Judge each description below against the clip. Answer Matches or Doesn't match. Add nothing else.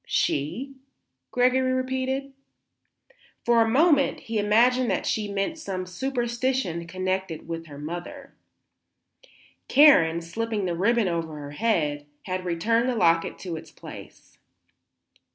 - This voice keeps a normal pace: Doesn't match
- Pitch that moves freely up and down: Matches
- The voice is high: Matches